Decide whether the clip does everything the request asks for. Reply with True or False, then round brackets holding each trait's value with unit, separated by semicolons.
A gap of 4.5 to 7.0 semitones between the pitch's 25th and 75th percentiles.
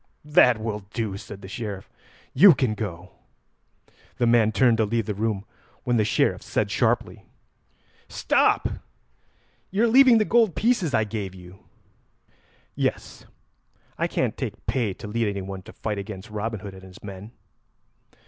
False (3.7 semitones)